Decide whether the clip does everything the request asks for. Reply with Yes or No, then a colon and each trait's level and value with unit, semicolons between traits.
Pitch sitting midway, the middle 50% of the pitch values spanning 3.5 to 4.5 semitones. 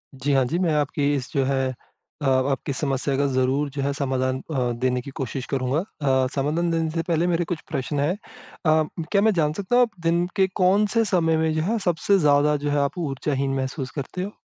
Yes: medium, 145 Hz; average, 3.9 semitones